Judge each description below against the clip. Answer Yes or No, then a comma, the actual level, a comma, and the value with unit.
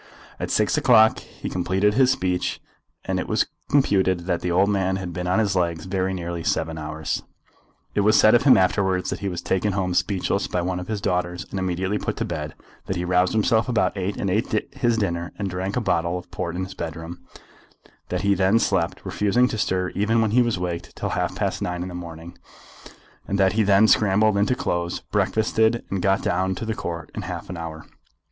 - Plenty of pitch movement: No, average, 2.8 semitones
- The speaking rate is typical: No, fast, 220 wpm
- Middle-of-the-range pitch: No, very low, 95 Hz